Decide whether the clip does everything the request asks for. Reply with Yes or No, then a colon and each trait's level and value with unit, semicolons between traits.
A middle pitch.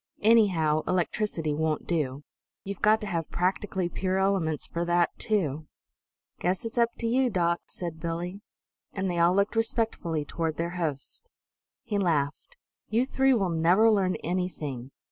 Yes: medium, 180 Hz